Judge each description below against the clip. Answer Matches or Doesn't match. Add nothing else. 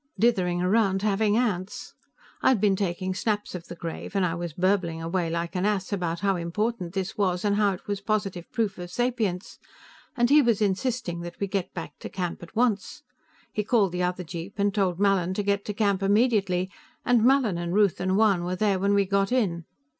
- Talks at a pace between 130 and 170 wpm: Doesn't match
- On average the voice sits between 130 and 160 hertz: Doesn't match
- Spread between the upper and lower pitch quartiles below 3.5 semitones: Matches